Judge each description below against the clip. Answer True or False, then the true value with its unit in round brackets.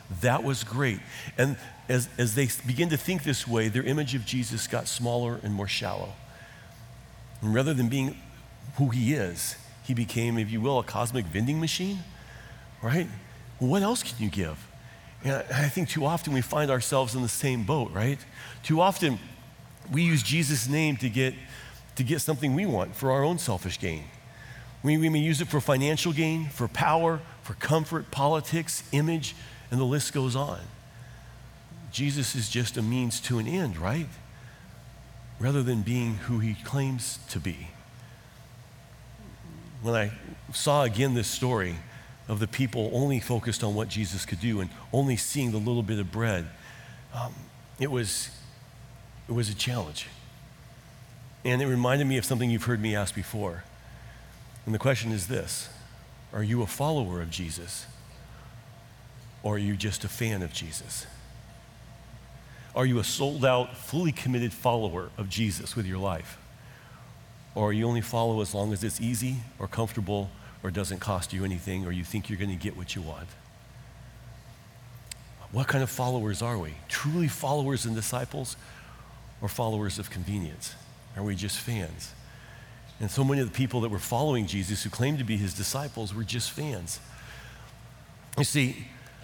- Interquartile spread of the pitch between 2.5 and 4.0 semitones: True (3.4 semitones)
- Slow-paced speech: False (170 wpm)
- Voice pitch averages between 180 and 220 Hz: False (120 Hz)